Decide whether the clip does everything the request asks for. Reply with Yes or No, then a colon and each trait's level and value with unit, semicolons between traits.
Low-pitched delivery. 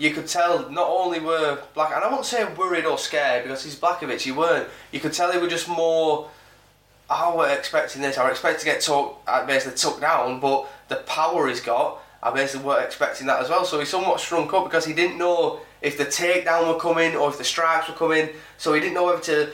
No: medium, 160 Hz